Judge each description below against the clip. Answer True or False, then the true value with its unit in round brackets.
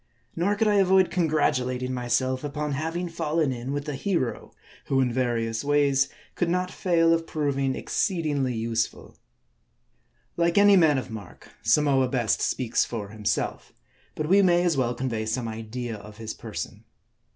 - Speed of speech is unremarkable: True (160 wpm)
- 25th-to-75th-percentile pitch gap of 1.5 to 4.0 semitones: False (5.5 semitones)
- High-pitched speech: False (135 Hz)